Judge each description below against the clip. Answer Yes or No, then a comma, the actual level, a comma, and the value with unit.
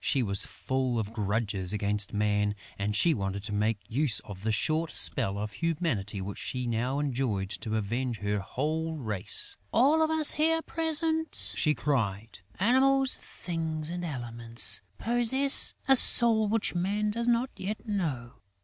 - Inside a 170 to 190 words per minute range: No, average, 155 wpm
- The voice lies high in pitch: No, low, 130 Hz